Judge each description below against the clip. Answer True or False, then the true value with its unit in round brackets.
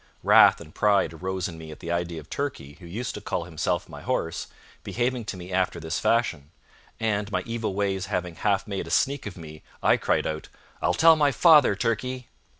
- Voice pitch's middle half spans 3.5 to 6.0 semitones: True (5.6 semitones)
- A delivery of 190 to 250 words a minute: True (205 wpm)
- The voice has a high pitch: False (95 Hz)